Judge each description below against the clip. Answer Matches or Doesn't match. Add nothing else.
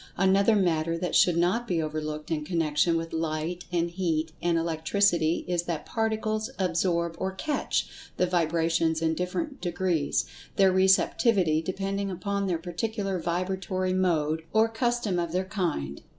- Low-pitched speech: Doesn't match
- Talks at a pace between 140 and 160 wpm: Matches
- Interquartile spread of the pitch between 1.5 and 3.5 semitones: Matches